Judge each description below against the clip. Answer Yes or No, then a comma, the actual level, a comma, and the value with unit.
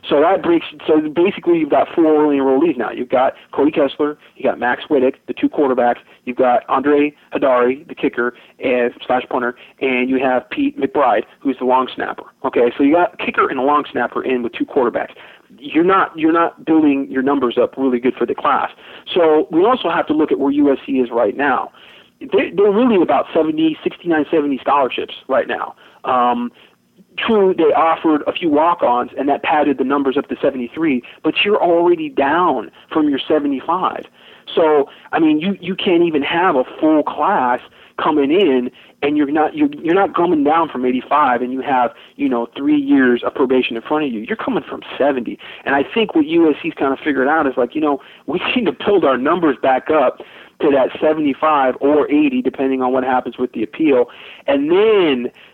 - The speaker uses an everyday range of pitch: No, wide, 7.3 semitones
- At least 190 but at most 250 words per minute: Yes, fast, 205 wpm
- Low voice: No, medium, 150 Hz